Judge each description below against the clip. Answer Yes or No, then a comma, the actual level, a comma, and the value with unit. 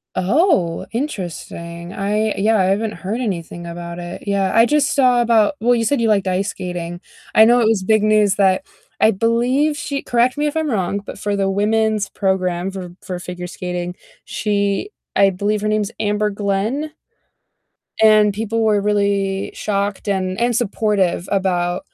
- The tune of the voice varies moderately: Yes, average, 3.1 semitones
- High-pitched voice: Yes, high, 205 Hz